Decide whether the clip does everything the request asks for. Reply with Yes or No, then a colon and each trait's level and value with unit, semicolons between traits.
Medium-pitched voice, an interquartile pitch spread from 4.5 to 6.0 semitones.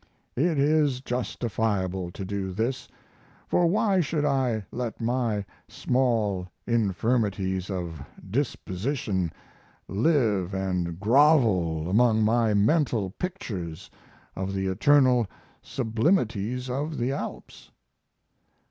No: low, 115 Hz; wide, 5.6 semitones